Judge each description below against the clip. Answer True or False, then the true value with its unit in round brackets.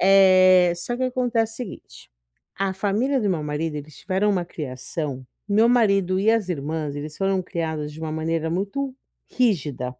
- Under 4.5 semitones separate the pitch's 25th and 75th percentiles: False (5.1 semitones)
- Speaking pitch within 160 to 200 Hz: True (185 Hz)